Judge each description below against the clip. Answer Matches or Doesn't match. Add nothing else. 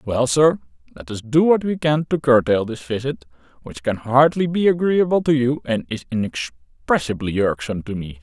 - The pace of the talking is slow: Doesn't match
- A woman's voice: Doesn't match